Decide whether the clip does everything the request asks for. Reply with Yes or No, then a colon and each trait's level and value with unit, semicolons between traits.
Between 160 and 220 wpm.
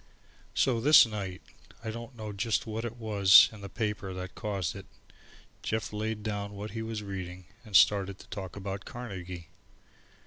Yes: average, 170 wpm